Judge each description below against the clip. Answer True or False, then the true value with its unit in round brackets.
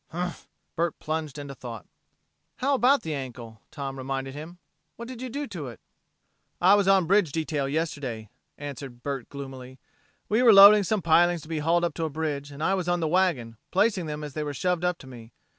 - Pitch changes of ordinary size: True (4.9 semitones)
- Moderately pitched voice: True (155 Hz)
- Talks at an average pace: False (210 wpm)